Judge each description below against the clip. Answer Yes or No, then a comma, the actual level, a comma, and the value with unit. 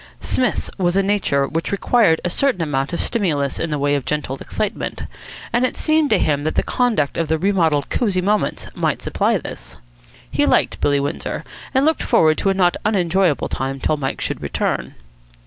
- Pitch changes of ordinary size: No, wide, 6.0 semitones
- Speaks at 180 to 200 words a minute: Yes, average, 190 wpm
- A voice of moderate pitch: Yes, medium, 170 Hz